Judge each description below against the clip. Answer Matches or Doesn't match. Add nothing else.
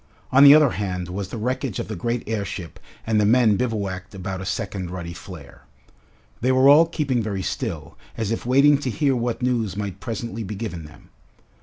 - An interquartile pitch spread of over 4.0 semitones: Matches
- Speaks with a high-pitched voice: Doesn't match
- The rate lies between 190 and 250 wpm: Matches